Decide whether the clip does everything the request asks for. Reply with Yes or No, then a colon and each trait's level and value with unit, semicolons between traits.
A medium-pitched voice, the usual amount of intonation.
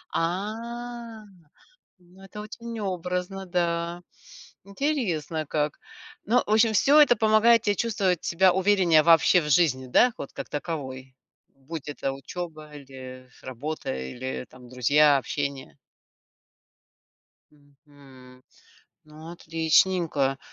No: medium, 165 Hz; wide, 6.1 semitones